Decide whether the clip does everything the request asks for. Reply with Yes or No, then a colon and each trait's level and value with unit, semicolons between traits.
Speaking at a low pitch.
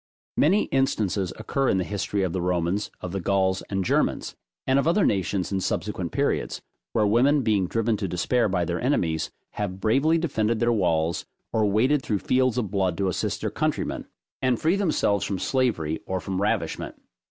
Yes: low, 105 Hz